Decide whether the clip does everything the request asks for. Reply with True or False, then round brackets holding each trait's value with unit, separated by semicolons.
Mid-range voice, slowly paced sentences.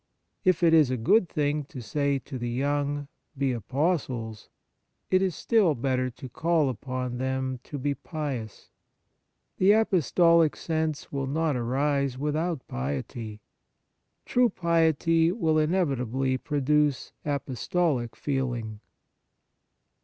True (145 Hz; 120 wpm)